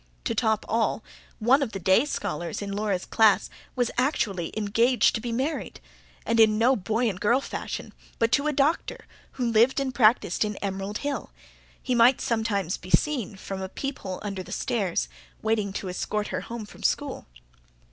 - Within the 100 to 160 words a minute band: No, average, 175 wpm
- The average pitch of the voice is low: No, high, 220 Hz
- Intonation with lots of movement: No, average, 3.8 semitones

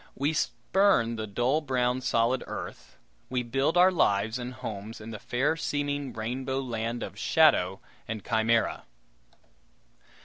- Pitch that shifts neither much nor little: Yes, average, 3.8 semitones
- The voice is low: Yes, low, 125 Hz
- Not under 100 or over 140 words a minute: Yes, slow, 135 wpm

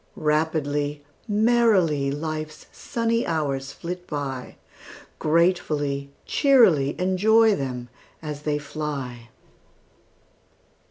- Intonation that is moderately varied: Yes, average, 4.4 semitones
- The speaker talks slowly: Yes, slow, 75 wpm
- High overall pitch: No, medium, 155 Hz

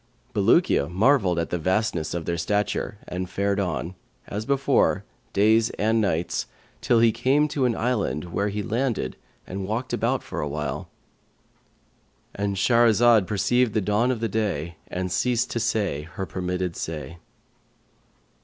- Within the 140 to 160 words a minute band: Yes, average, 145 wpm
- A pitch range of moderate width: Yes, average, 4.3 semitones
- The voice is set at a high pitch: No, low, 100 Hz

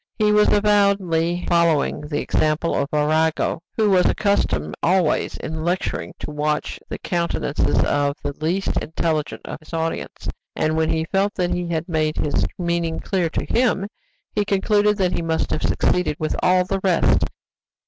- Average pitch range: Yes, average, 3.6 semitones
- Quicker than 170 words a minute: No, average, 165 wpm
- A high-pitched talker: No, medium, 170 Hz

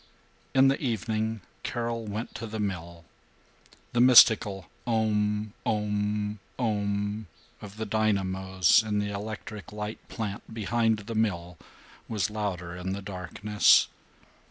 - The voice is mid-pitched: No, low, 105 Hz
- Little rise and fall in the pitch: Yes, narrow, 1.8 semitones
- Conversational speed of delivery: No, slow, 120 wpm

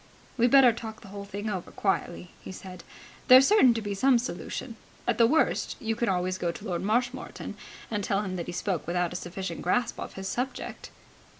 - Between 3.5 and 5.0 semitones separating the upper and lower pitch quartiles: Yes, average, 4.5 semitones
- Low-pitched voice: No, high, 205 Hz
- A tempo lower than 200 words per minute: No, fast, 205 wpm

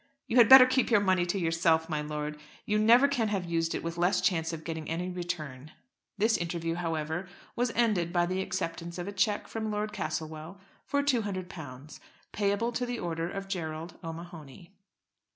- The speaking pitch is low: No, medium, 175 Hz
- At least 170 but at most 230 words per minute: Yes, average, 180 wpm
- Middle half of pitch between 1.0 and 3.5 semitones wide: No, average, 4.1 semitones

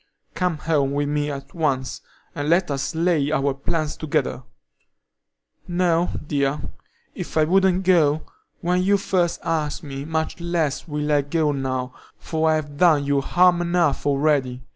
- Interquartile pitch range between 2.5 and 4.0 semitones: Yes, average, 3.3 semitones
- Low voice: No, medium, 155 Hz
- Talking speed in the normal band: Yes, average, 150 wpm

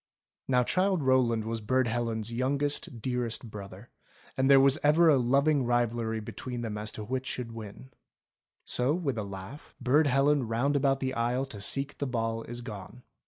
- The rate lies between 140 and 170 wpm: No, average, 185 wpm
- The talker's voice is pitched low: Yes, low, 125 Hz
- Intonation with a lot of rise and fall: No, average, 3.3 semitones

